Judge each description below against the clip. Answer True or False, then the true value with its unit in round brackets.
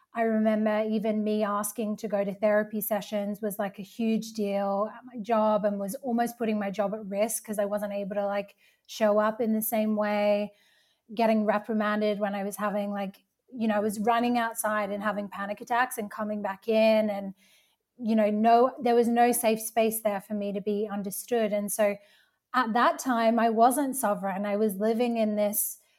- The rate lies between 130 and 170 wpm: False (200 wpm)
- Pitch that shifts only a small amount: True (1.5 semitones)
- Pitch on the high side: True (215 Hz)